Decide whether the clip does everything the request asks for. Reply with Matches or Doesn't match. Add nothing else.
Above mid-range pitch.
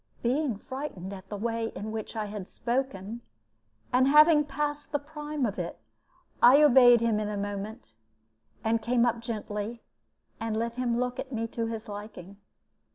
Matches